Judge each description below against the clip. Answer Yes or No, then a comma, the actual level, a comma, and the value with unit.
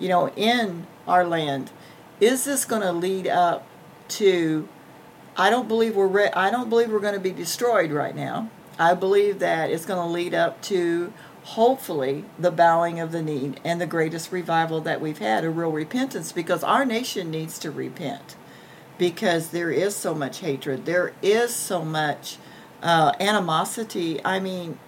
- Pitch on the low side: No, medium, 175 Hz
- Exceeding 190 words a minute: No, average, 170 wpm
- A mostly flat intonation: No, average, 3.8 semitones